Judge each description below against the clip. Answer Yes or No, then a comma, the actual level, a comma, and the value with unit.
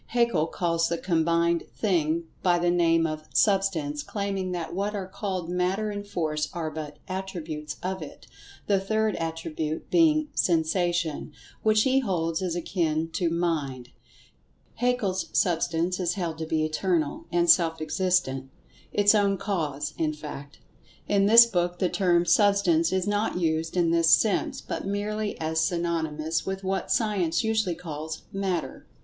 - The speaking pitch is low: No, medium, 175 Hz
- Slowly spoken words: No, average, 145 wpm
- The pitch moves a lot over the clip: No, average, 3.4 semitones